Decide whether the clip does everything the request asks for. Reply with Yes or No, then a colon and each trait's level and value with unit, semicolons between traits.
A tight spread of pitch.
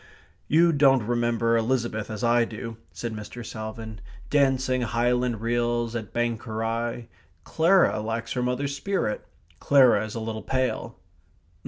Yes: narrow, 2.2 semitones